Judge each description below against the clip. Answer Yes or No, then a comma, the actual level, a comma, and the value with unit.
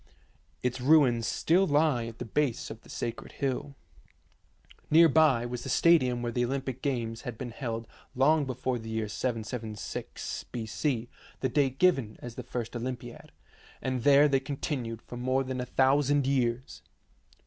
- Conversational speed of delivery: Yes, average, 160 wpm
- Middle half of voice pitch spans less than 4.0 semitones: Yes, average, 2.9 semitones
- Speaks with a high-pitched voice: No, low, 125 Hz